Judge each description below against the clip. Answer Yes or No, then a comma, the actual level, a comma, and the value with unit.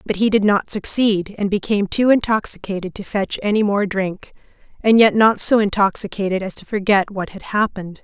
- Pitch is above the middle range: Yes, high, 200 Hz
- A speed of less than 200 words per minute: Yes, average, 185 wpm